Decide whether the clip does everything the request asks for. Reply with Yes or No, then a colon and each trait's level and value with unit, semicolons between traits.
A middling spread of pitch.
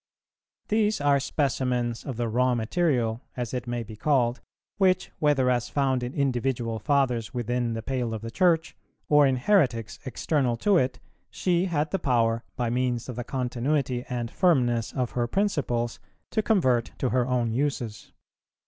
Yes: average, 3.3 semitones